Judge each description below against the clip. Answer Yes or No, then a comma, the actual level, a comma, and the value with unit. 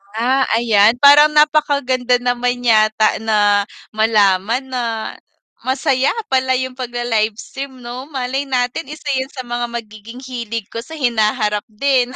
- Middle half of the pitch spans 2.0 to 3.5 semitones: Yes, average, 2.9 semitones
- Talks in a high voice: Yes, high, 245 Hz